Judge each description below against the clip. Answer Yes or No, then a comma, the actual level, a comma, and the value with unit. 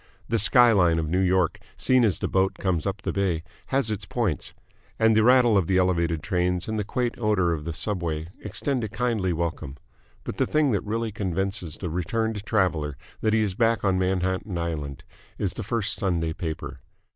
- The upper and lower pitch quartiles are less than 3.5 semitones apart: No, average, 4.4 semitones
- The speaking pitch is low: Yes, very low, 95 Hz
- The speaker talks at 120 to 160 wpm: No, average, 195 wpm